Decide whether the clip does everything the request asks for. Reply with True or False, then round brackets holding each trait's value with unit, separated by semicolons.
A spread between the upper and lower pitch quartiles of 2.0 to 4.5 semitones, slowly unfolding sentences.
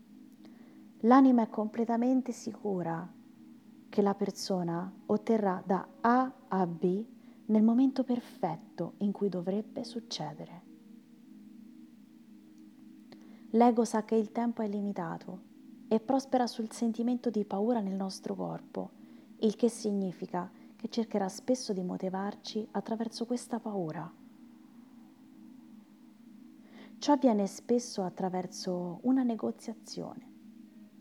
True (3.5 semitones; 100 wpm)